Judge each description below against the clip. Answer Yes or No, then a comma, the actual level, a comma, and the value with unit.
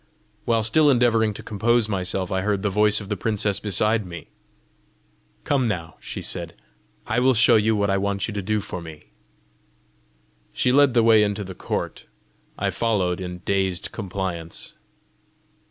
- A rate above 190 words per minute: No, average, 165 wpm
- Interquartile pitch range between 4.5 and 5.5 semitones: No, average, 3.0 semitones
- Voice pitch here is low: Yes, low, 105 Hz